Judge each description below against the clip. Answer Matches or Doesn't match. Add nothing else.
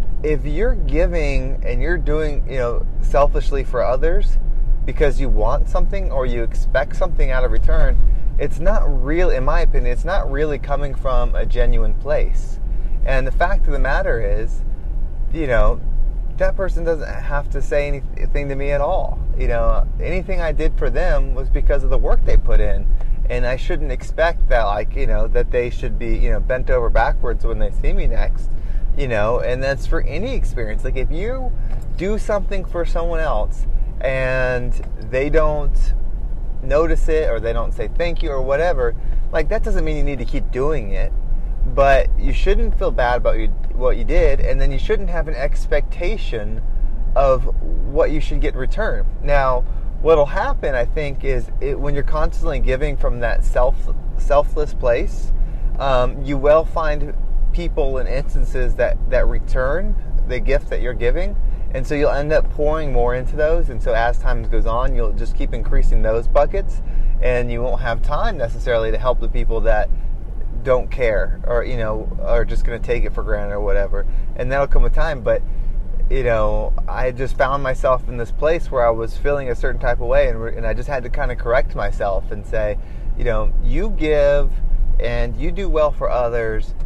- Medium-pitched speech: Doesn't match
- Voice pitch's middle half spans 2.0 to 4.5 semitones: Matches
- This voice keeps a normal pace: Matches